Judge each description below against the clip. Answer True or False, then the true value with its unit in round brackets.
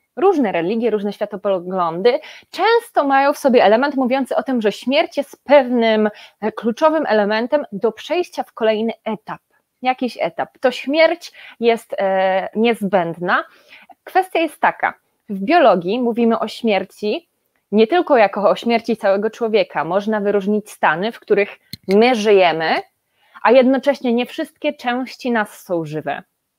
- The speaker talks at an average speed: True (135 wpm)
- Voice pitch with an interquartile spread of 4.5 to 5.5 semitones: True (4.8 semitones)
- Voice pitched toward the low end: False (230 Hz)